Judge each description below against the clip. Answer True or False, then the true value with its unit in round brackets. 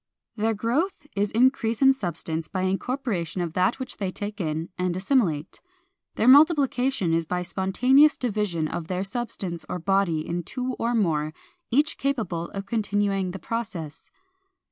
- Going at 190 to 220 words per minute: False (150 wpm)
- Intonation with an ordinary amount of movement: False (5.8 semitones)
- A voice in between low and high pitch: False (200 Hz)